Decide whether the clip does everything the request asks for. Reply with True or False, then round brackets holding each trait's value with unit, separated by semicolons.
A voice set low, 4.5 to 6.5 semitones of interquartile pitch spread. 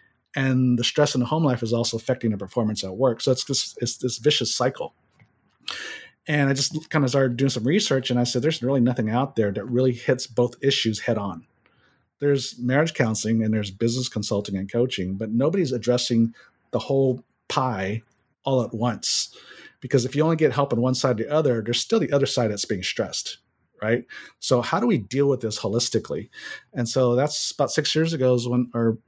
False (125 Hz; 2.9 semitones)